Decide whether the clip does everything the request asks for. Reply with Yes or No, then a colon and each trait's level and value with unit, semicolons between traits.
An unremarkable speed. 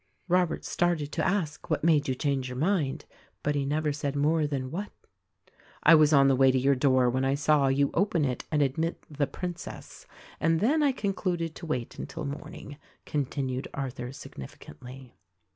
Yes: average, 175 wpm